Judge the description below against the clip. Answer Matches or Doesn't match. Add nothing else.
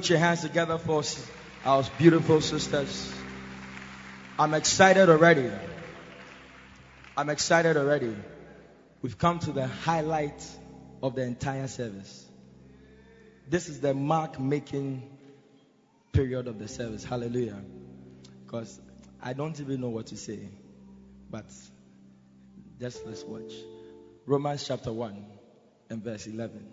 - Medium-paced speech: Doesn't match